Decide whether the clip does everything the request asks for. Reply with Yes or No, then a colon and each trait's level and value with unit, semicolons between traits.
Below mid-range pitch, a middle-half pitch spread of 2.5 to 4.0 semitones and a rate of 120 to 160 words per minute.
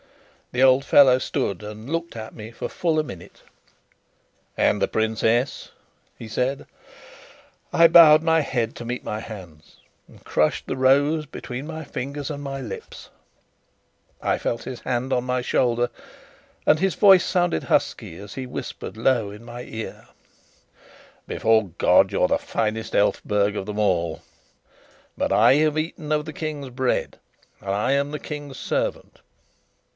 No: low, 130 Hz; average, 5.1 semitones; average, 155 wpm